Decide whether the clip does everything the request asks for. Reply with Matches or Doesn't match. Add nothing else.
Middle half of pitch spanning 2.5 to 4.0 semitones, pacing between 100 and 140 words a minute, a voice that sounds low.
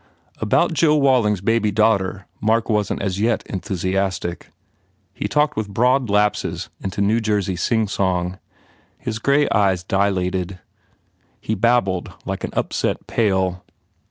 Matches